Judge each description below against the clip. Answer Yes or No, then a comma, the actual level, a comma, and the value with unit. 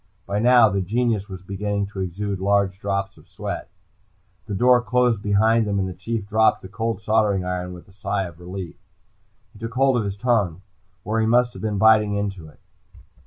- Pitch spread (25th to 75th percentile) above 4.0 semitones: No, average, 2.7 semitones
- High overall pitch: No, low, 100 Hz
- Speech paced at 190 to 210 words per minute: Yes, average, 200 wpm